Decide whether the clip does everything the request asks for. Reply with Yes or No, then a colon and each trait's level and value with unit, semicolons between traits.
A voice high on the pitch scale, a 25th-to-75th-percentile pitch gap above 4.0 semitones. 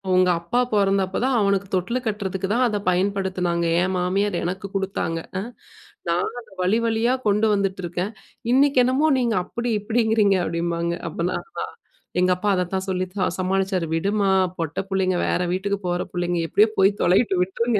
No: high, 195 Hz; narrow, 2.5 semitones